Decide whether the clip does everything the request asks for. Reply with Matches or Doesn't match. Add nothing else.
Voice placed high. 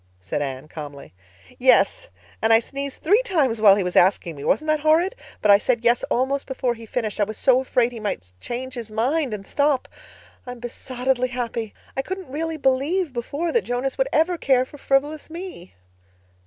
Matches